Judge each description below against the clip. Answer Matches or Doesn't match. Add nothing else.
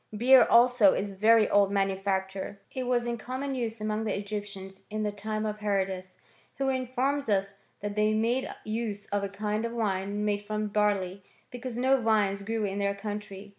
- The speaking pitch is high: Matches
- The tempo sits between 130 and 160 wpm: Doesn't match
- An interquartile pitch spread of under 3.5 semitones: Matches